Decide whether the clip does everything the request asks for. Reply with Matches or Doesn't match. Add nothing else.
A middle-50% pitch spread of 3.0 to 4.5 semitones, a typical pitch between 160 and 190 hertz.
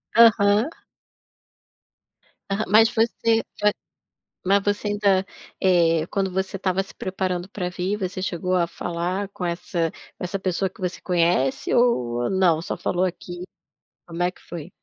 Doesn't match